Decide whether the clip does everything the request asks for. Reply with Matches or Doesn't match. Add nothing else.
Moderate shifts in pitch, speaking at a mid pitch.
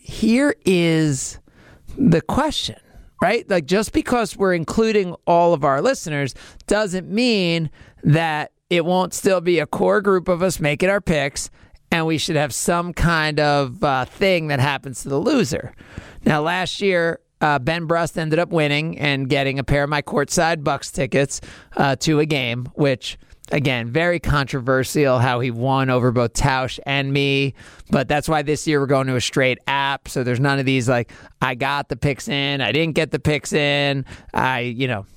Matches